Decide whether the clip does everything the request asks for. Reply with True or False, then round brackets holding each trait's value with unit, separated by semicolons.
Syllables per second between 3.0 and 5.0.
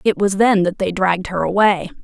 False (5.5 syllables/s)